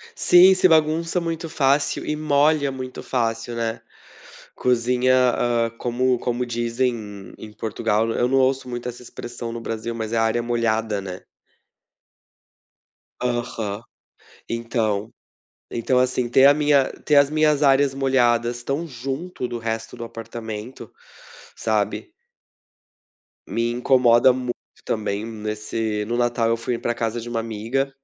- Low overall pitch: Yes, low, 120 Hz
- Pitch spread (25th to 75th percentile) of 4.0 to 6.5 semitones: No, average, 2.8 semitones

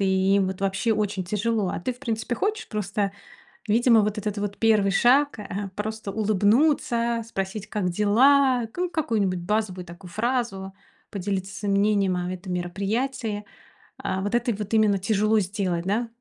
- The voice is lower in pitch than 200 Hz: No, high, 210 Hz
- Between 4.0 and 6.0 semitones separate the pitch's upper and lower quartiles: No, average, 3.0 semitones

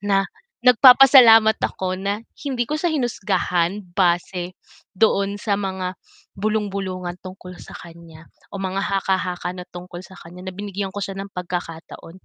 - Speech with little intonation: Yes, narrow, 2.3 semitones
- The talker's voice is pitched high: Yes, high, 195 Hz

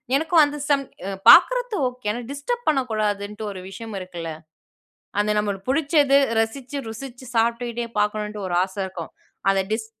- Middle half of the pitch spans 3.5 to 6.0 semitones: Yes, average, 4.9 semitones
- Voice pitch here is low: No, high, 225 Hz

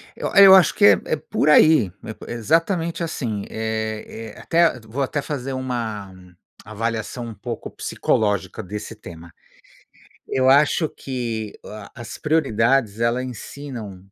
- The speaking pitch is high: No, low, 120 Hz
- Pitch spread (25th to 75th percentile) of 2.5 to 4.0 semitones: No, average, 4.6 semitones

